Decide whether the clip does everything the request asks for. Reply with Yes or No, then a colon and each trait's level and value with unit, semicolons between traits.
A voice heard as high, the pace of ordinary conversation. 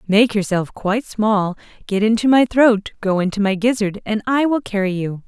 Yes: high, 210 Hz; average, 180 wpm